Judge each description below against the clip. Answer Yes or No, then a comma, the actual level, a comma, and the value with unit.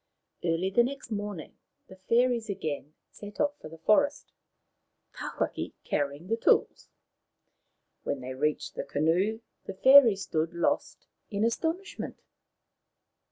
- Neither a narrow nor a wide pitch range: No, wide, 6.7 semitones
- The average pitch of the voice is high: Yes, high, 200 Hz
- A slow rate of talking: Yes, slow, 120 wpm